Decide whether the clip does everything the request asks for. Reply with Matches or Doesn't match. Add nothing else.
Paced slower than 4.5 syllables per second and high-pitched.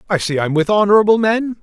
Doesn't match